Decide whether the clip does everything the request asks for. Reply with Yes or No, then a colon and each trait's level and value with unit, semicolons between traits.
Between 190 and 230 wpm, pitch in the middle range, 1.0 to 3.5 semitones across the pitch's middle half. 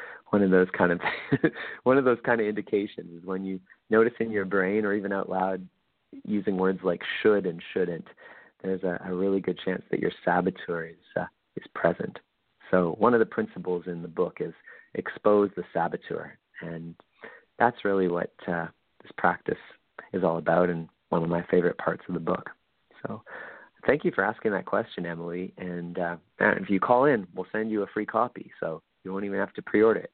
No: average, 200 wpm; very low, 95 Hz; average, 2.8 semitones